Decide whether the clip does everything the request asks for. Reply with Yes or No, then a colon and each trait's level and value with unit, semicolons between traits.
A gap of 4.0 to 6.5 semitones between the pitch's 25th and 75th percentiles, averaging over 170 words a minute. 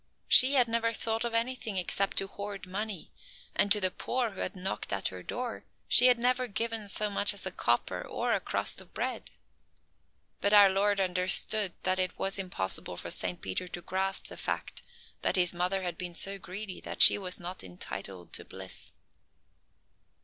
No: average, 3.2 semitones; average, 185 wpm